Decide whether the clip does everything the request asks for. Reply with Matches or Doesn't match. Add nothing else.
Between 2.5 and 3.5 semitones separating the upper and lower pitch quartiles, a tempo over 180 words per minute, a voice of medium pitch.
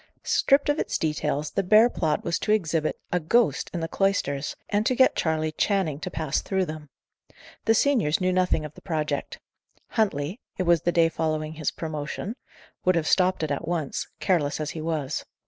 Doesn't match